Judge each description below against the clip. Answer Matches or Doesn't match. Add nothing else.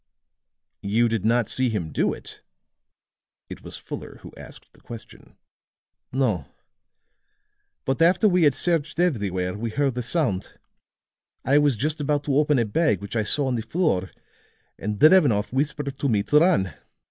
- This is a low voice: Matches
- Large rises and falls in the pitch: Matches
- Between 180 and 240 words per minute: Doesn't match